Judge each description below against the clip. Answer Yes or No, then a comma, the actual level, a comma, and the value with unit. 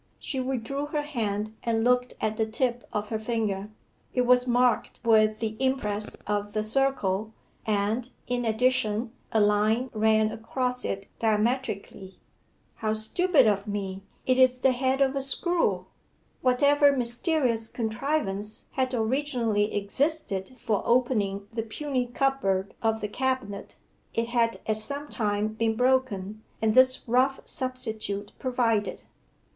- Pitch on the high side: Yes, high, 230 Hz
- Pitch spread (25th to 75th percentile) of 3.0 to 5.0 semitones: Yes, average, 3.3 semitones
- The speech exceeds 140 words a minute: No, slow, 135 wpm